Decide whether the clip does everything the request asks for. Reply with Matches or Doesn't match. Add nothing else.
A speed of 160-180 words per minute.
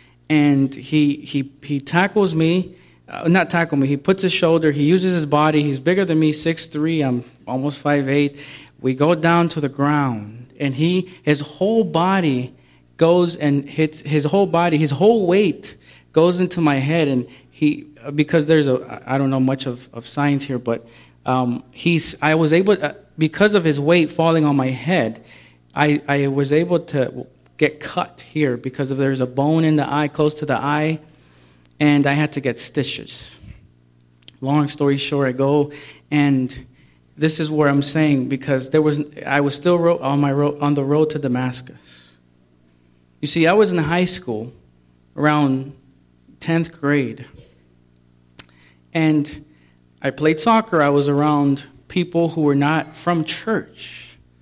Matches